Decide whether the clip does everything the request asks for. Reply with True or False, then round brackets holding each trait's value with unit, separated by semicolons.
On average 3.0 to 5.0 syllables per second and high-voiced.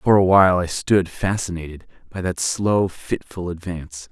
False (4.7 syllables/s; 90 Hz)